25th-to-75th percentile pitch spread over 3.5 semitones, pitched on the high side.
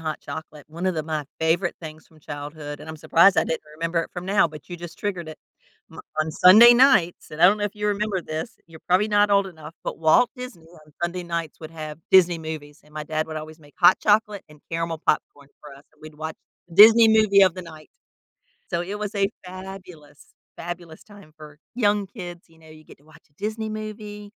No: average, 4.1 semitones; medium, 170 Hz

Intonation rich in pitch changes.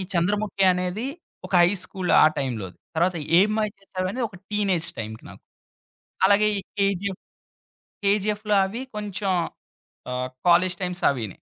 No: average, 3.0 semitones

